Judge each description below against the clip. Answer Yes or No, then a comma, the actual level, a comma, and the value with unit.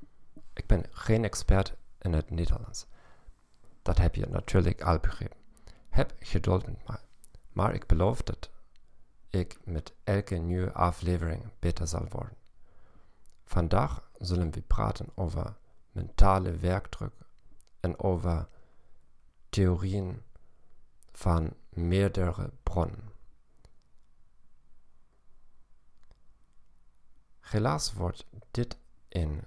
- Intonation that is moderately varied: Yes, average, 3.9 semitones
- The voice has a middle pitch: No, very low, 90 Hz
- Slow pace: Yes, slow, 95 wpm